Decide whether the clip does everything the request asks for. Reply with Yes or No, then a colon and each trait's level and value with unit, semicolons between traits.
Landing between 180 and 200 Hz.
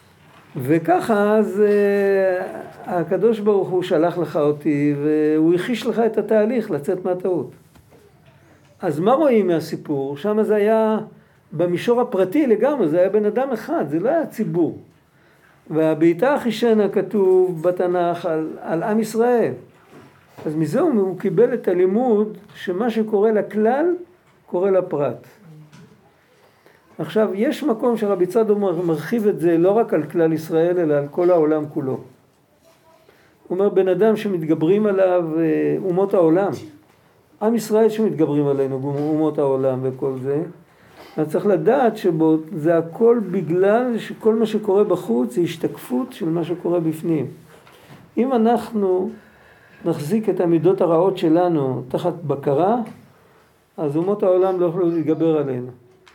Yes: medium, 185 Hz